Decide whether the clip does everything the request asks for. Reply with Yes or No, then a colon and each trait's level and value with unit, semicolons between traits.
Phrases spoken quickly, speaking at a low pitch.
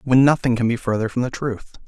Yes: fast, 255 wpm; low, 125 Hz